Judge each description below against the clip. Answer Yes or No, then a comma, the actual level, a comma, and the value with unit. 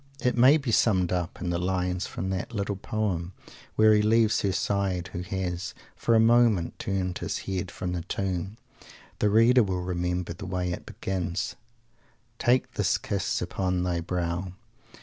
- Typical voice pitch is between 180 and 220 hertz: No, very low, 95 Hz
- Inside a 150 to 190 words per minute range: Yes, average, 170 wpm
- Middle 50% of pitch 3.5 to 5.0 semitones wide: No, average, 3.0 semitones